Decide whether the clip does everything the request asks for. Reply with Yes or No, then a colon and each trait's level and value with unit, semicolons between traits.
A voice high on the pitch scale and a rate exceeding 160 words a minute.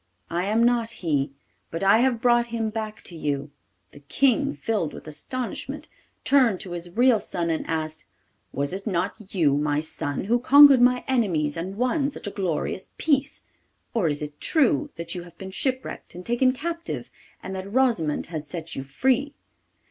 Yes: high, 195 Hz; average, 180 wpm